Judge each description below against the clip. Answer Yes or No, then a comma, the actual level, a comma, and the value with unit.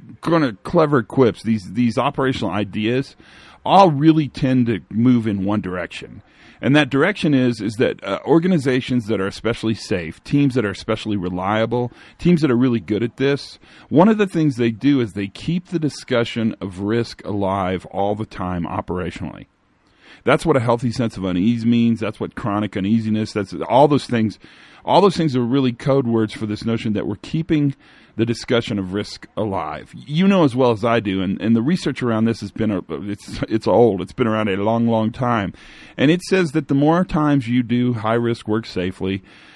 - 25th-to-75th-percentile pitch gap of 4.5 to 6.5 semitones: Yes, average, 4.8 semitones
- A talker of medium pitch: No, low, 115 Hz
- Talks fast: No, average, 195 wpm